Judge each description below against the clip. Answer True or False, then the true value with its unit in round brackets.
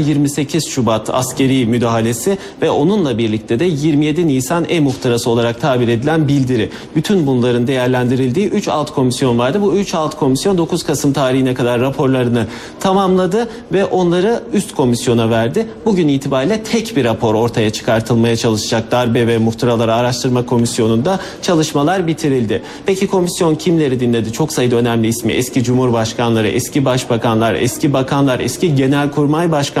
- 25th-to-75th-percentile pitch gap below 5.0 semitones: False (5.3 semitones)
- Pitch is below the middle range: True (130 Hz)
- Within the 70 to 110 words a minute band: False (140 wpm)